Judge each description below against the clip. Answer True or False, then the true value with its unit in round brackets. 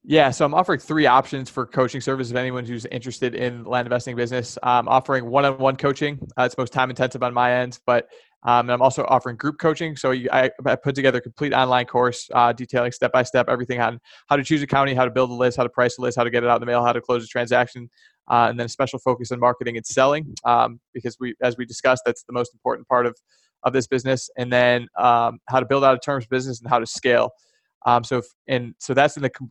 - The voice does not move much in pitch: True (1.4 semitones)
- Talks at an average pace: False (265 wpm)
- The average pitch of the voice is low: True (125 Hz)